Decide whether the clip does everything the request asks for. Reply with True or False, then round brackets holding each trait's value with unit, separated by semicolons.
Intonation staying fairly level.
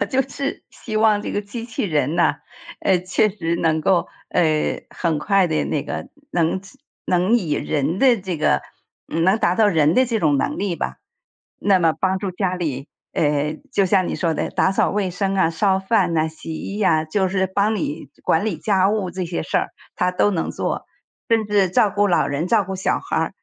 False (3.9 semitones)